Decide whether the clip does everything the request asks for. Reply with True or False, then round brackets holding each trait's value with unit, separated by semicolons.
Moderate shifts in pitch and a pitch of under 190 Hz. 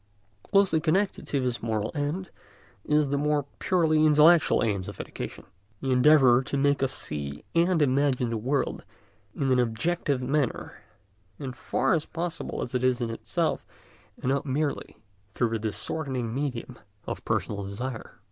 True (3.9 semitones; 135 Hz)